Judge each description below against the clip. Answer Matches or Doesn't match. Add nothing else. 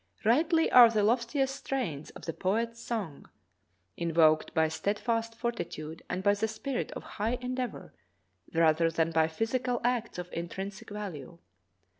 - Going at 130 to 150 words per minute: Matches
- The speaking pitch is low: Doesn't match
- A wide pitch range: Matches